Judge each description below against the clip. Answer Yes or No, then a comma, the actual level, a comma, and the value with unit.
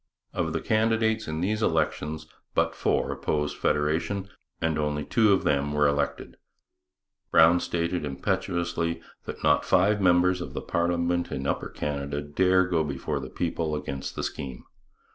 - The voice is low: Yes, very low, 85 Hz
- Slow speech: No, average, 145 wpm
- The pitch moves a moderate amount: Yes, average, 3.6 semitones